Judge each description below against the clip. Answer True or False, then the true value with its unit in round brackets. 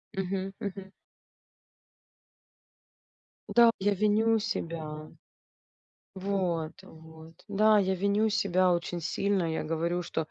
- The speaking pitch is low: False (190 Hz)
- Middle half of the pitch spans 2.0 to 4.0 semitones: True (3.5 semitones)